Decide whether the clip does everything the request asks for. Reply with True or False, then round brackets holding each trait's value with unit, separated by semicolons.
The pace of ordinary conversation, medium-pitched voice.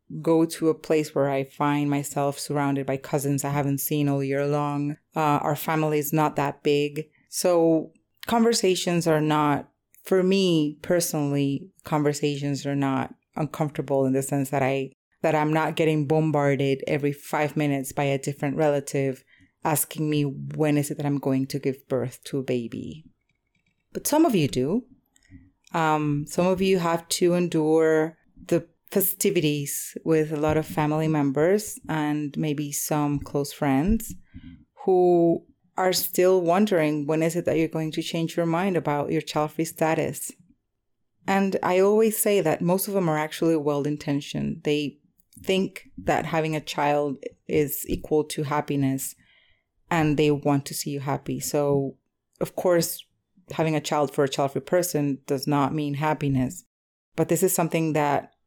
True (160 wpm; 150 Hz)